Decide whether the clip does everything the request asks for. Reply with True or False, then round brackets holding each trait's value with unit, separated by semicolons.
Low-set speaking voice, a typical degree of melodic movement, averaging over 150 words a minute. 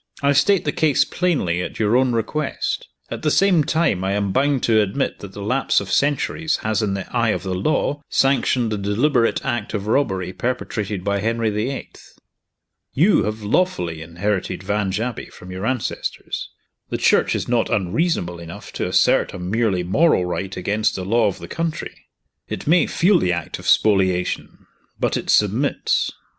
False (110 Hz; 6.5 semitones; 175 wpm)